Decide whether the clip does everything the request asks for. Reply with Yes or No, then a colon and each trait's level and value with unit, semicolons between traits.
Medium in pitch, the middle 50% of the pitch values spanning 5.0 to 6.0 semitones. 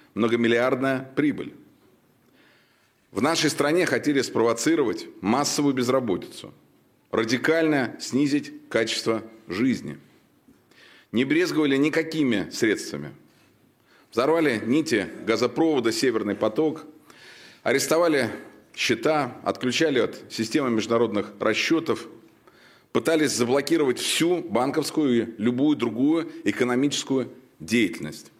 Yes: medium, 145 Hz; average, 5.3 semitones